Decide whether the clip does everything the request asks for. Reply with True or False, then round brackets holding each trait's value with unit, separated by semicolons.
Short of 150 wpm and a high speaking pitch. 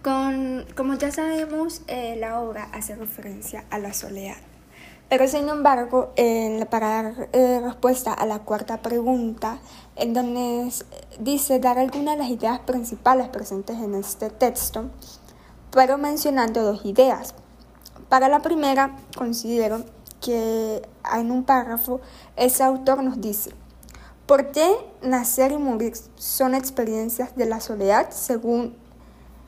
True (130 wpm; 245 Hz)